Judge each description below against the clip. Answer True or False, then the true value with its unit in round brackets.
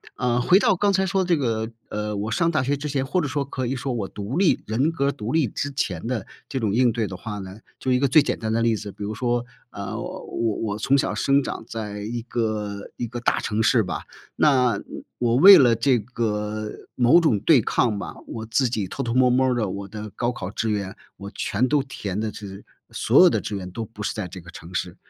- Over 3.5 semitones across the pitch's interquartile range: True (4.1 semitones)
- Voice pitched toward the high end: False (115 Hz)